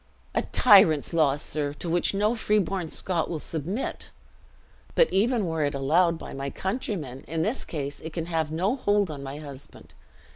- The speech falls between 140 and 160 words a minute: No, average, 175 wpm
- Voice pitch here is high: No, medium, 165 Hz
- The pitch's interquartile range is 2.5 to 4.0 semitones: No, average, 5.1 semitones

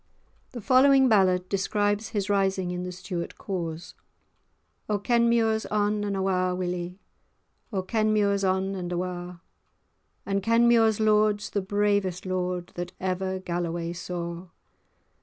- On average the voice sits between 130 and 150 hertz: No, high, 190 Hz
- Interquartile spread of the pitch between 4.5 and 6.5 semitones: No, average, 2.7 semitones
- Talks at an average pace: No, slow, 120 wpm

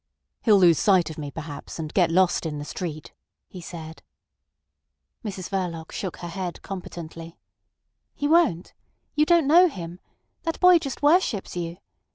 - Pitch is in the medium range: Yes, medium, 180 Hz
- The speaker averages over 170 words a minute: No, average, 155 wpm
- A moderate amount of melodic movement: No, wide, 7.4 semitones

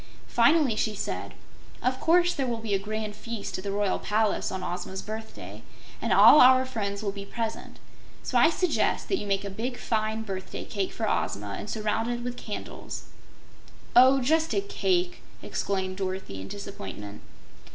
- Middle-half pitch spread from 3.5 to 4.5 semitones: Yes, average, 3.8 semitones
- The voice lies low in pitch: No, high, 215 Hz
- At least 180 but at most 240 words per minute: No, average, 170 wpm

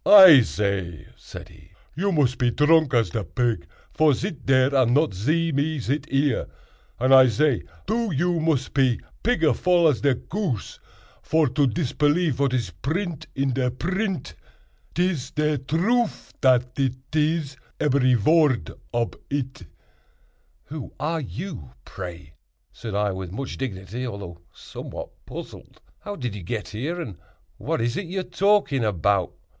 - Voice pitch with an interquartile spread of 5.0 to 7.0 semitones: Yes, wide, 5.4 semitones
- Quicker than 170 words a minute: No, average, 150 wpm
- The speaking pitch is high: No, low, 135 Hz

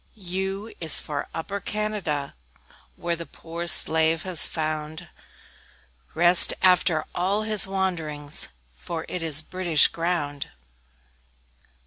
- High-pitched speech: No, medium, 170 Hz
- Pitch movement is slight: No, average, 3.1 semitones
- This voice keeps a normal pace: No, slow, 110 wpm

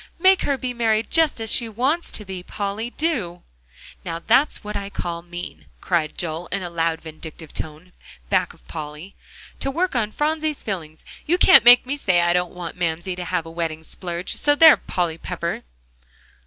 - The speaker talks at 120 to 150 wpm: No, average, 185 wpm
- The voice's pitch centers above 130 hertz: Yes, medium, 185 Hz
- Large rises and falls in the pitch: Yes, wide, 6.6 semitones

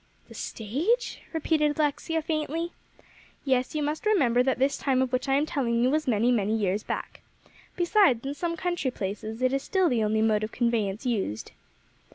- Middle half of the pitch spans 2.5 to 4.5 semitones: No, wide, 5.5 semitones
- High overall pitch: Yes, very high, 260 Hz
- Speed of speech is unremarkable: Yes, average, 185 wpm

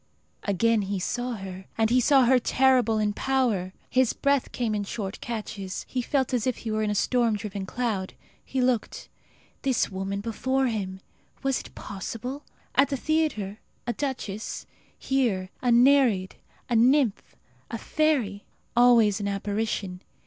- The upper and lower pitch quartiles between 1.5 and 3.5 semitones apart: No, average, 4.2 semitones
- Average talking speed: Yes, average, 150 wpm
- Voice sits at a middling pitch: No, high, 230 Hz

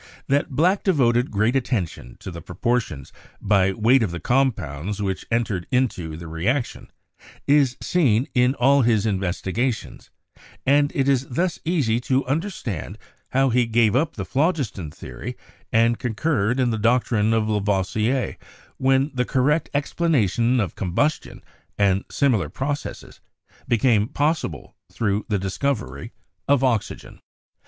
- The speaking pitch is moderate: No, low, 120 Hz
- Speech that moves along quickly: No, average, 140 wpm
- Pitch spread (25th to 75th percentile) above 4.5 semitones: Yes, average, 5.1 semitones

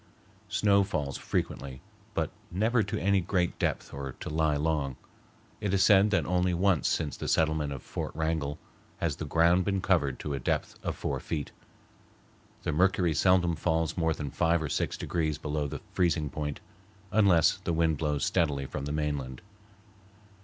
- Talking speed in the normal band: Yes, average, 170 wpm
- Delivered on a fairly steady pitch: No, average, 3.7 semitones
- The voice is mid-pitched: No, very low, 80 Hz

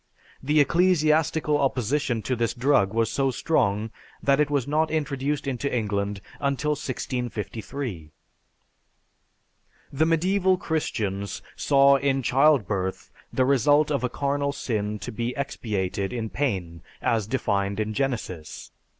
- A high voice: No, low, 130 Hz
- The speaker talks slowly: Yes, slow, 125 wpm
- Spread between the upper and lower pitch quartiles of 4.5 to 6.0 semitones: Yes, average, 5.3 semitones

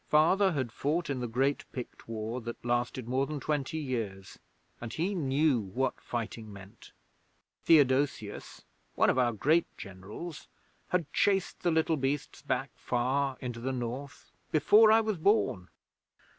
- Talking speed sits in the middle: Yes, average, 145 wpm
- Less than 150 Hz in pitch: Yes, low, 135 Hz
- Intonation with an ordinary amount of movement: Yes, average, 4.7 semitones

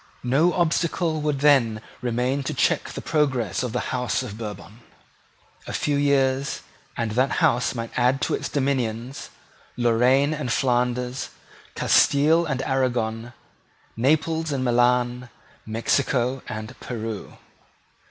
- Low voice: Yes, low, 125 Hz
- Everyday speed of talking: No, slow, 125 wpm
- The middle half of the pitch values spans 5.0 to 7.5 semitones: No, average, 2.9 semitones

